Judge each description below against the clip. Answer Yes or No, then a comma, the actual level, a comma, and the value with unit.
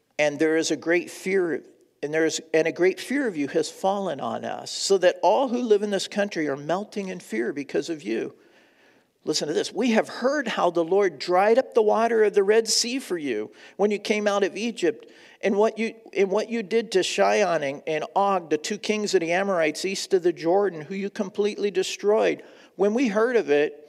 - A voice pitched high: Yes, high, 200 Hz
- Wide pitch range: No, average, 4.7 semitones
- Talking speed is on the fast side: Yes, fast, 225 wpm